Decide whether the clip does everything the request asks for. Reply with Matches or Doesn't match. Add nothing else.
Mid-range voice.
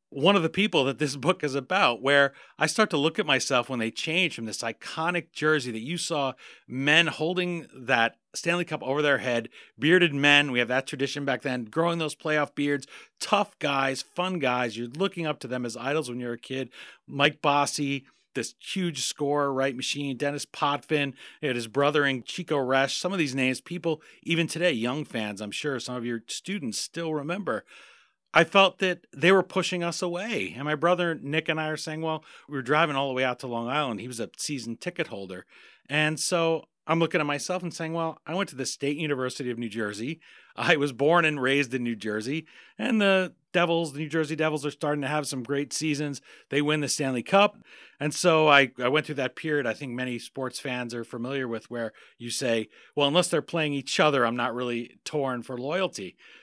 Matches